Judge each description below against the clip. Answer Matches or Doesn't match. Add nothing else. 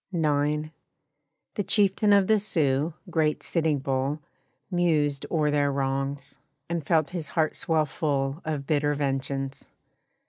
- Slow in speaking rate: Matches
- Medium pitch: Matches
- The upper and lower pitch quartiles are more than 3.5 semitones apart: Doesn't match